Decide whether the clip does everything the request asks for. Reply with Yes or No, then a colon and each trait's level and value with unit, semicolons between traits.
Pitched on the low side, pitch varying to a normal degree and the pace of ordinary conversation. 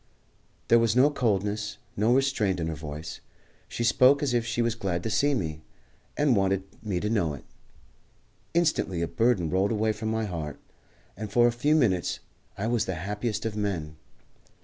Yes: low, 105 Hz; average, 4.4 semitones; average, 180 wpm